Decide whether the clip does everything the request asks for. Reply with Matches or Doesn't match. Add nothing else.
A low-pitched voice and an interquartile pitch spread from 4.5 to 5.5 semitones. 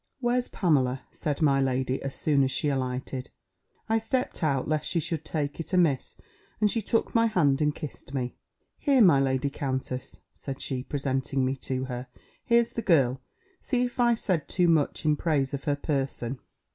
Doesn't match